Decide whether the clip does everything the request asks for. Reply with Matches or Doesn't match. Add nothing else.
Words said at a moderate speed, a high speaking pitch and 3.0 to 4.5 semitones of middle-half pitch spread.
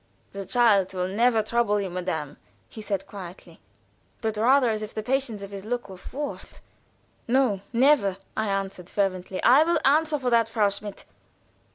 Matches